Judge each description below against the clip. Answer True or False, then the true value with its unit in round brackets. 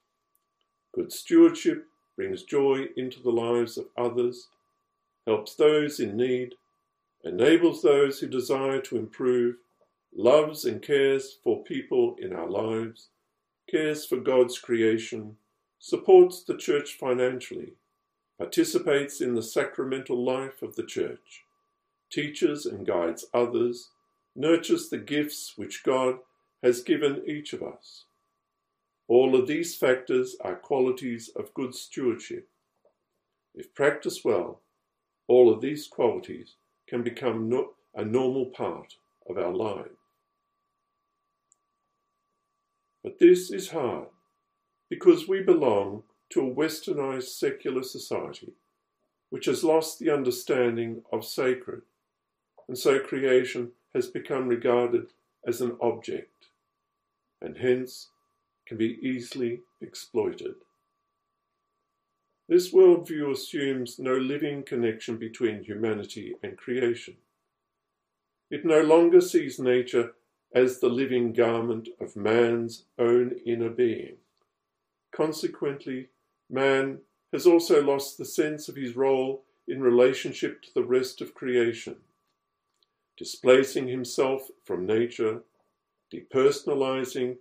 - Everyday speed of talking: False (110 wpm)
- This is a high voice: False (150 Hz)